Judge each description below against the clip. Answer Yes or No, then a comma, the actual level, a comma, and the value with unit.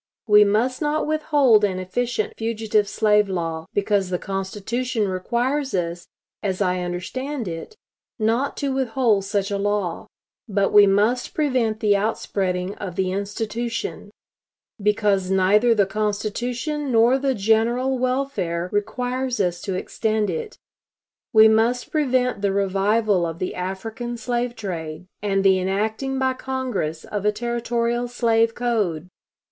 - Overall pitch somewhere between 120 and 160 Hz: No, high, 215 Hz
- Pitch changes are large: No, average, 4.0 semitones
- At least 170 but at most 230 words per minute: No, slow, 135 wpm